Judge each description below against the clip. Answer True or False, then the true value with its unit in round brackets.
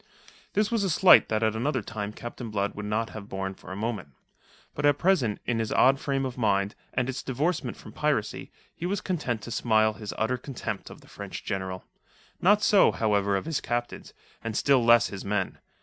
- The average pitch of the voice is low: True (115 Hz)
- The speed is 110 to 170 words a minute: False (200 wpm)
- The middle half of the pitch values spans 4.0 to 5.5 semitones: True (4.7 semitones)